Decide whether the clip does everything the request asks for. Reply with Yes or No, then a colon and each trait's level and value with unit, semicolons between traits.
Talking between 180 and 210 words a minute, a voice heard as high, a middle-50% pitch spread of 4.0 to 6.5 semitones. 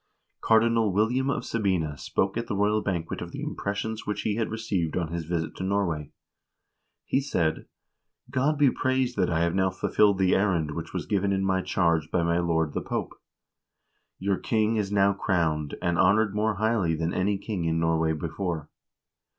No: average, 185 wpm; very low, 95 Hz; average, 4.4 semitones